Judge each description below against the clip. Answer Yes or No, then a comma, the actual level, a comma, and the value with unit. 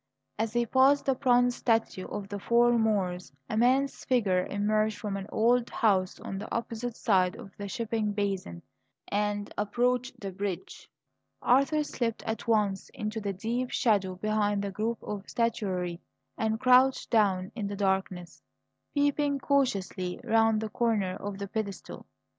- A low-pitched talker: No, high, 215 Hz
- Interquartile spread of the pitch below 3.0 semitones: No, average, 3.3 semitones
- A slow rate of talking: No, average, 155 wpm